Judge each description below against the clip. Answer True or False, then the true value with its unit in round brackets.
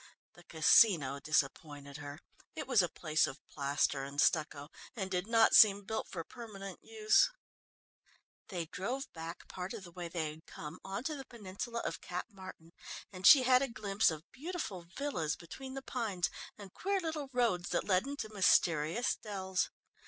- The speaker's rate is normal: True (170 wpm)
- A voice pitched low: False (190 Hz)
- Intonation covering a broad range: True (6.3 semitones)